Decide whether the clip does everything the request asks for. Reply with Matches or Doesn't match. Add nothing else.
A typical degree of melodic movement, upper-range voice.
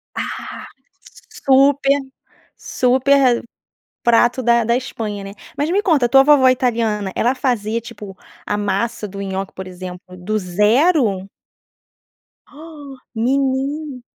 Matches